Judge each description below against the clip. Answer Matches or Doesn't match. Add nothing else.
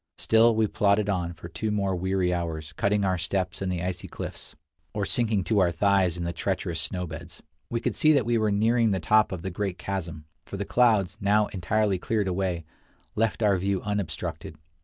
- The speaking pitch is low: Matches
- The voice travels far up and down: Doesn't match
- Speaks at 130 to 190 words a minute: Doesn't match